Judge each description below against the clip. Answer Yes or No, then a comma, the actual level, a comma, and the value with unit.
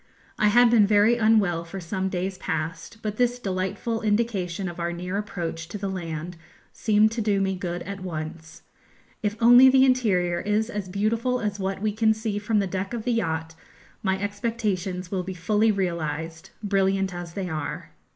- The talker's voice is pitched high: Yes, high, 195 Hz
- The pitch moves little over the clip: No, average, 3.5 semitones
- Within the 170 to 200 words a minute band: Yes, average, 180 wpm